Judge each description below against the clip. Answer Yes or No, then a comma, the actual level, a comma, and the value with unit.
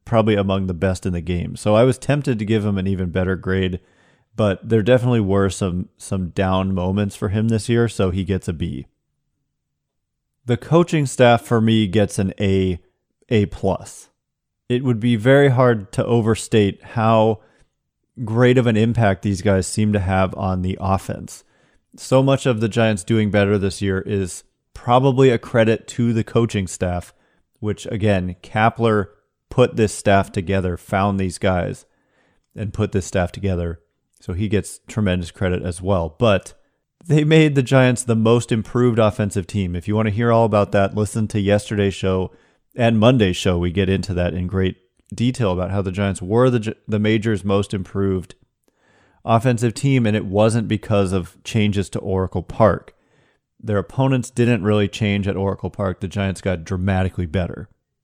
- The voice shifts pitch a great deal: No, average, 3.4 semitones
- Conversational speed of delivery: Yes, average, 175 wpm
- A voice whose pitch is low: Yes, low, 105 Hz